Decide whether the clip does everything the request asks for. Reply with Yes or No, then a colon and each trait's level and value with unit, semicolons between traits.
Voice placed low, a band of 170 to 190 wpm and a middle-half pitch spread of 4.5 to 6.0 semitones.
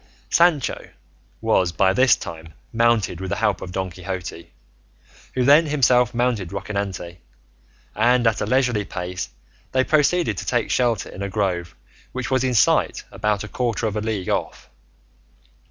No: low, 110 Hz; average, 155 wpm; average, 4.9 semitones